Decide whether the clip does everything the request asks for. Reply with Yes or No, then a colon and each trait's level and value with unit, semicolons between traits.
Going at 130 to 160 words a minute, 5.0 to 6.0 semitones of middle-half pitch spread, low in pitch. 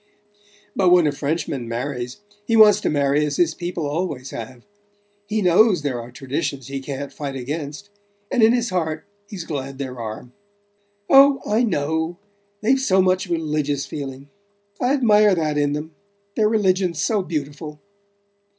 No: average, 155 wpm; wide, 5.6 semitones; medium, 155 Hz